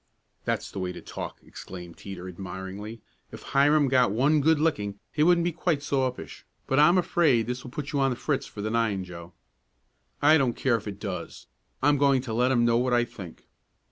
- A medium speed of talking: No, fast, 210 wpm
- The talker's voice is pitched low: Yes, low, 125 Hz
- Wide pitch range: Yes, wide, 6.0 semitones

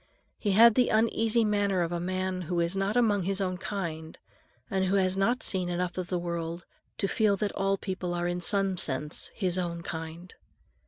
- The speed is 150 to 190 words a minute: No, average, 200 wpm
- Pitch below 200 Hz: Yes, medium, 185 Hz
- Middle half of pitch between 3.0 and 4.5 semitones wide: No, narrow, 2.5 semitones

